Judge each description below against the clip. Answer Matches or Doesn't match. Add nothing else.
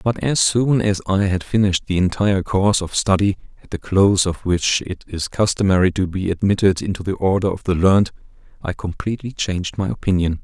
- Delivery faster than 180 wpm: Matches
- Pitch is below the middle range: Matches